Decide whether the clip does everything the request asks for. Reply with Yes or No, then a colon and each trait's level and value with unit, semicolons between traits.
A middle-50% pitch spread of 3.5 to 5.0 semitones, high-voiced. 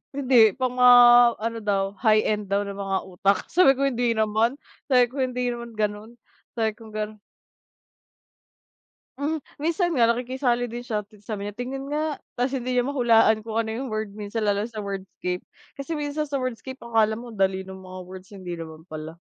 Yes: average, 3.8 semitones; high, 225 Hz